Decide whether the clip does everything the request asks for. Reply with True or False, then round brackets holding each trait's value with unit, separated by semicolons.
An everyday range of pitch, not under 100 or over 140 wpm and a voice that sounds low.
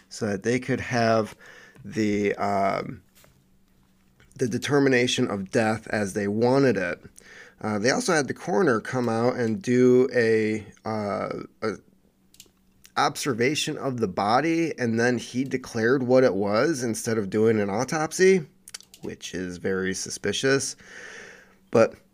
True (4.0 semitones; 135 wpm; 115 Hz)